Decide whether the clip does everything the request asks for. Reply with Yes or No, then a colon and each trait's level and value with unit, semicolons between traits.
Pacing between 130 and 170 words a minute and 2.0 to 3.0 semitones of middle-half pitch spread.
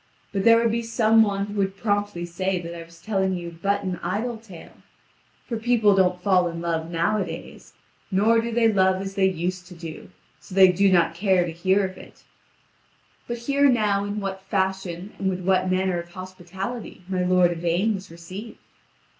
No: average, 190 wpm; narrow, 2.6 semitones